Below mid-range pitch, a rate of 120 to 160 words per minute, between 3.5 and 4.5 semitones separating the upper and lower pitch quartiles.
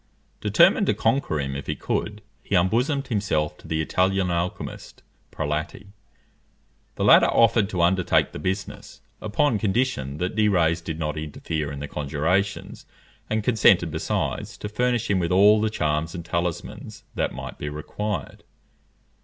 No: very low, 90 Hz; average, 155 wpm; average, 5.2 semitones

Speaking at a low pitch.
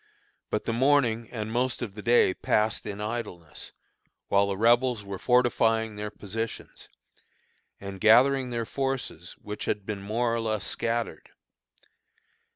Yes: low, 110 Hz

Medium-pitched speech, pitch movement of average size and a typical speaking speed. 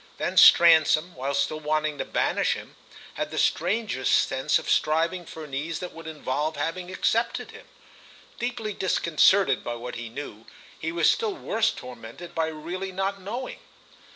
Yes: medium, 160 Hz; average, 4.5 semitones; average, 160 wpm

